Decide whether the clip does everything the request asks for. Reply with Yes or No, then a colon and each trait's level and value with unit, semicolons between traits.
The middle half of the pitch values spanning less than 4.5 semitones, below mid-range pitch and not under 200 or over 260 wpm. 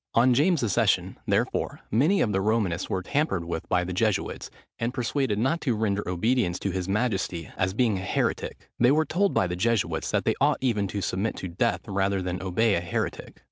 No: average, 4.8 semitones; low, 100 Hz; fast, 205 wpm